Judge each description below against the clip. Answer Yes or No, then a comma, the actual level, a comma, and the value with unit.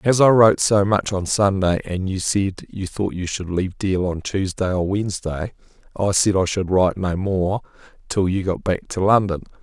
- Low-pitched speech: Yes, very low, 95 Hz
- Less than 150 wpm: No, average, 195 wpm